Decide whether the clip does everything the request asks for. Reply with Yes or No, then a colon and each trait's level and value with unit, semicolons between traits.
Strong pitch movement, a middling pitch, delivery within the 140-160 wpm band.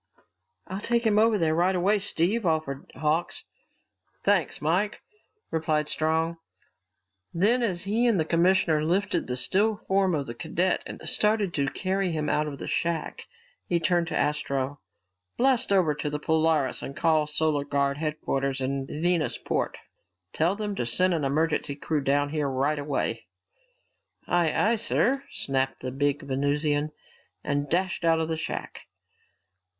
No: average, 4.5 semitones; medium, 160 Hz; average, 155 wpm